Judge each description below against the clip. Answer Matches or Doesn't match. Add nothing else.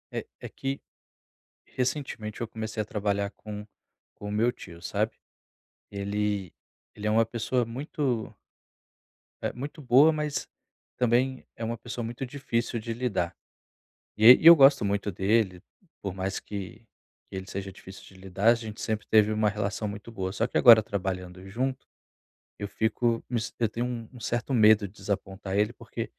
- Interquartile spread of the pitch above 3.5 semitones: Doesn't match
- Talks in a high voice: Doesn't match